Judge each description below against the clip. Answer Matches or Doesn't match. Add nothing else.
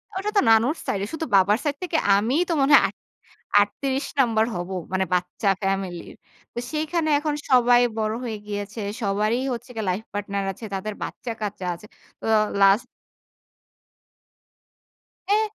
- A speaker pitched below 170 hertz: Doesn't match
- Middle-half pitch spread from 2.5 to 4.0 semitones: Doesn't match